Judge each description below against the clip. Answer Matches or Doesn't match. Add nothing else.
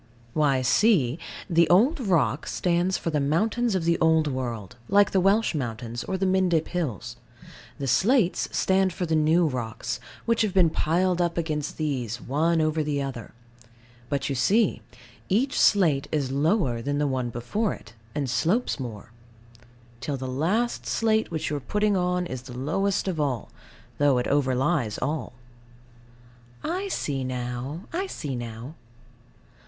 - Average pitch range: Doesn't match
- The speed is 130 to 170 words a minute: Matches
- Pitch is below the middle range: Doesn't match